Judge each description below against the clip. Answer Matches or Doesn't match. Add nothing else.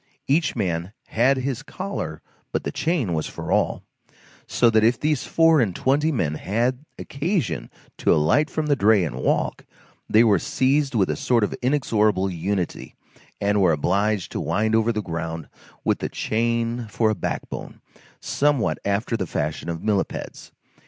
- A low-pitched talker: Matches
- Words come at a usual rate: Matches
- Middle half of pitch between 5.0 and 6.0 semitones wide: Matches